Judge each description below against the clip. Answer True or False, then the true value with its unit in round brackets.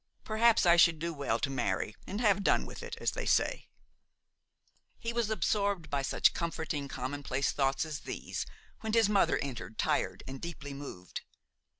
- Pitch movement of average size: False (6.9 semitones)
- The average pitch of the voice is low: False (160 Hz)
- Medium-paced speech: True (170 wpm)